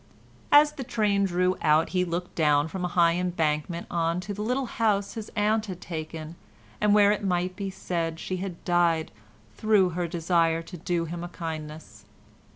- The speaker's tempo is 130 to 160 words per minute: No, average, 180 wpm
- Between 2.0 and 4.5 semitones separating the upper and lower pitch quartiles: Yes, average, 3.3 semitones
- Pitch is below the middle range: No, medium, 175 Hz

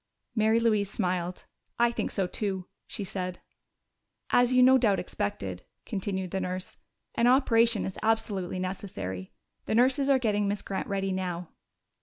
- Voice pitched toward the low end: No, high, 200 Hz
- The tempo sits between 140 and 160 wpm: Yes, average, 150 wpm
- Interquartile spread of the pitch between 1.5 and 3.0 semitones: No, average, 4.0 semitones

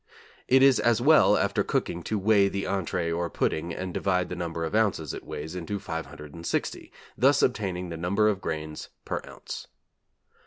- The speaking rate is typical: Yes, average, 170 wpm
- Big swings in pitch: No, average, 4.2 semitones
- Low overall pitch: Yes, very low, 90 Hz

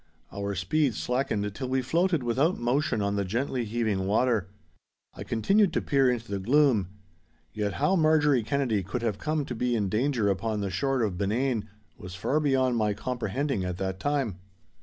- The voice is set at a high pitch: No, low, 120 Hz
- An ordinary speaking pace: Yes, average, 180 wpm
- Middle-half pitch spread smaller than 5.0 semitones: No, average, 5.3 semitones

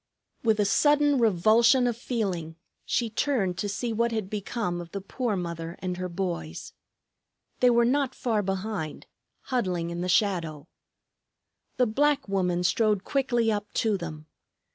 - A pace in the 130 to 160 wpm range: Yes, average, 150 wpm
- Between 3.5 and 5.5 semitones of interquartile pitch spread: Yes, average, 4.9 semitones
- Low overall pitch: No, high, 205 Hz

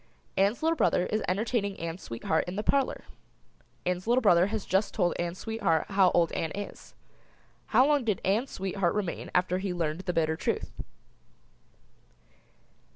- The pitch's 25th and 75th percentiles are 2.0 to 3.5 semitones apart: No, average, 3.9 semitones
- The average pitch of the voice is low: No, high, 190 Hz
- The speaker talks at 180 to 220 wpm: No, average, 160 wpm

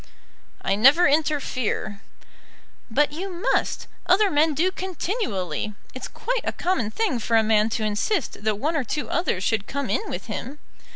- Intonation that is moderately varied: No, wide, 8.3 semitones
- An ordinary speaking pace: Yes, average, 165 wpm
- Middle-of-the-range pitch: No, very high, 280 Hz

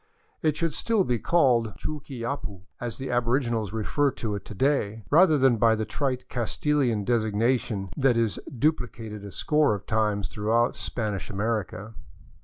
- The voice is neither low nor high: No, low, 115 Hz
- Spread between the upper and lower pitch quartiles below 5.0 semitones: Yes, average, 4.0 semitones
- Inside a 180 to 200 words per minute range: No, average, 150 wpm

